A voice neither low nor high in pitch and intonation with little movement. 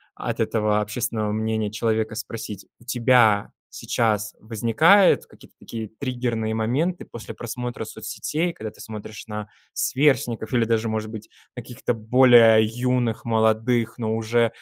No: low, 115 Hz; narrow, 1.9 semitones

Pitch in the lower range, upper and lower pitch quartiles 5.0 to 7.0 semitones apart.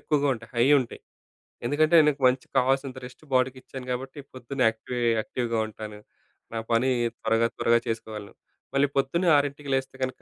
No: low, 130 Hz; average, 2.9 semitones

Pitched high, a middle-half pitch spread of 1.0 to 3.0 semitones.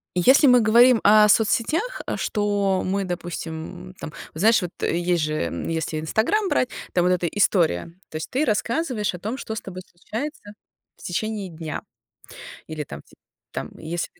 No: high, 195 Hz; average, 4.8 semitones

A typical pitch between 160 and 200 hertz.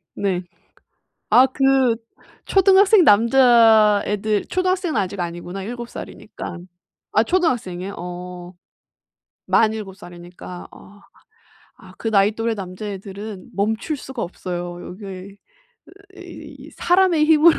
No: high, 210 Hz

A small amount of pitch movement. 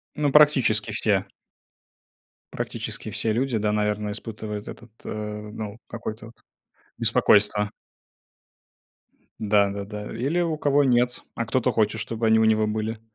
Yes: narrow, 2.1 semitones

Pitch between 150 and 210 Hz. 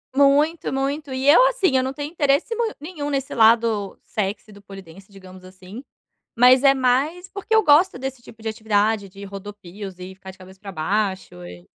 No: high, 225 Hz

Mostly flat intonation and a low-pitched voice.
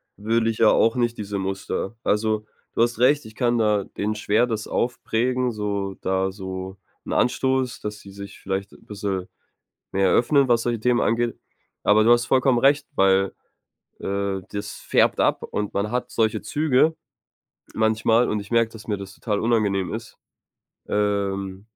No: average, 3.1 semitones; low, 110 Hz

